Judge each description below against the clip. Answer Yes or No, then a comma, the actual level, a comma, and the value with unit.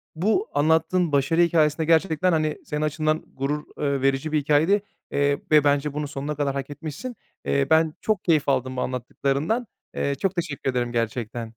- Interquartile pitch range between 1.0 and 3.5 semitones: Yes, average, 2.8 semitones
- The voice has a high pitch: No, medium, 150 Hz